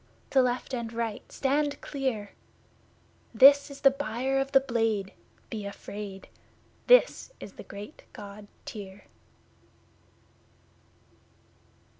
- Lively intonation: No, average, 4.7 semitones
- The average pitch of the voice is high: Yes, high, 235 Hz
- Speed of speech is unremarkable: No, slow, 105 wpm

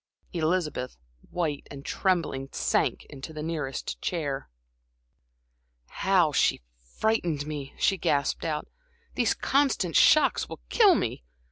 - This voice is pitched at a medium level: Yes, medium, 155 Hz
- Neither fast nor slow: No, slow, 115 wpm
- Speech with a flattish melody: No, average, 4.5 semitones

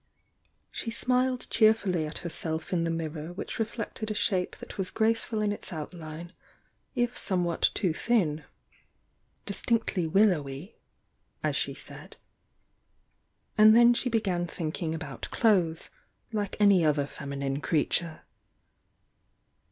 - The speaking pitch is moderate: Yes, medium, 180 Hz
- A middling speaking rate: No, slow, 130 wpm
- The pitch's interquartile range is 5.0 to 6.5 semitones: Yes, average, 5.3 semitones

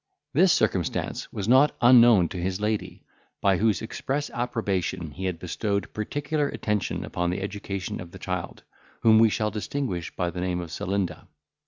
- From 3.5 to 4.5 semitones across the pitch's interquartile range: Yes, average, 4.0 semitones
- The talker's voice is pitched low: Yes, low, 100 Hz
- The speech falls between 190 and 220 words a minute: No, average, 165 wpm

